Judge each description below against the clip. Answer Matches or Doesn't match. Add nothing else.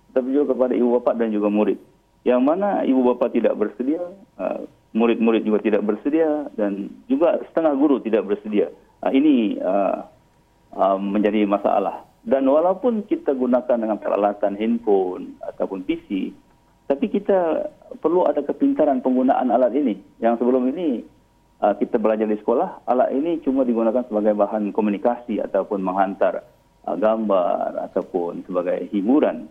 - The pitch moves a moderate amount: Doesn't match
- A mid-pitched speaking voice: Doesn't match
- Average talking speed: Matches